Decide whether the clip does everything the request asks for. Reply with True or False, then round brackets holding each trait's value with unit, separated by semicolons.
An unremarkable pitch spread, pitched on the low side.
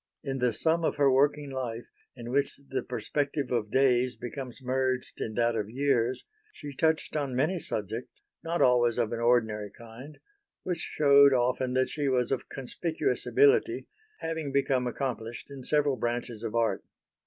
True (3.0 semitones; 130 Hz)